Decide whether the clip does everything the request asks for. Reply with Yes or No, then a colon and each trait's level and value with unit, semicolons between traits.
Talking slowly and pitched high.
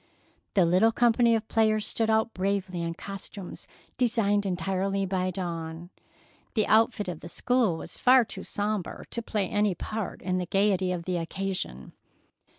No: average, 155 wpm; high, 195 Hz